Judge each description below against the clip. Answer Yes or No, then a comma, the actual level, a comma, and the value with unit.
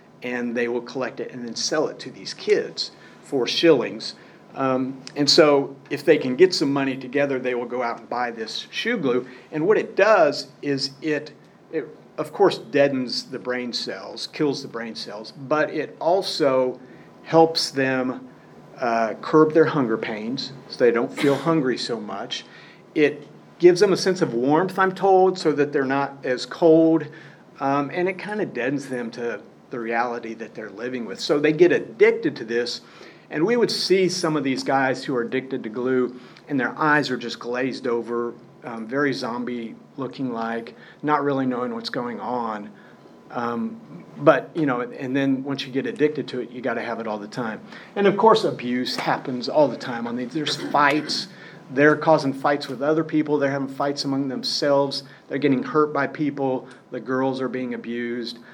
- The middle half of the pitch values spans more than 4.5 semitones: No, average, 3.5 semitones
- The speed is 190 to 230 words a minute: Yes, average, 195 wpm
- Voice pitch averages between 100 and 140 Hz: Yes, low, 135 Hz